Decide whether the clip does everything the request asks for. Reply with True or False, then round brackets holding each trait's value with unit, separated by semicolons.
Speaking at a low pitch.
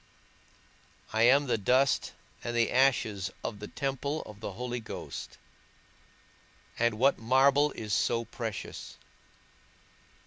True (120 Hz)